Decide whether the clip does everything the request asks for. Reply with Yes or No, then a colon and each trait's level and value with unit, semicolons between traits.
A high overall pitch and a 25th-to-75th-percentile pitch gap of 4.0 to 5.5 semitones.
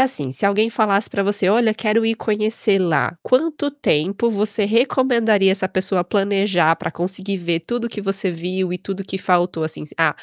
No: high, 200 Hz; average, 3.3 semitones